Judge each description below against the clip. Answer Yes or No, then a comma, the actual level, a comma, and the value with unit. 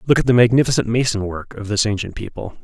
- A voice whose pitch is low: Yes, low, 115 Hz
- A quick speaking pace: Yes, fast, 230 wpm